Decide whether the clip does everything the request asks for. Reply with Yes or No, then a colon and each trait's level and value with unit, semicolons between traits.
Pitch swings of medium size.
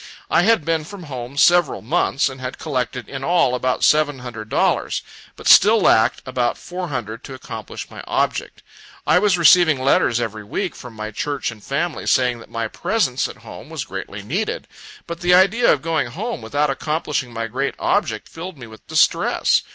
No: wide, 6.2 semitones